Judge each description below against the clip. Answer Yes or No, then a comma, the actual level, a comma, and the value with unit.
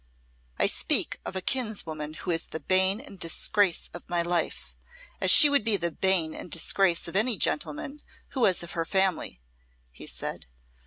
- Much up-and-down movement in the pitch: No, average, 3.5 semitones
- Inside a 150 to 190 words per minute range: Yes, average, 175 wpm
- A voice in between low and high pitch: Yes, medium, 180 Hz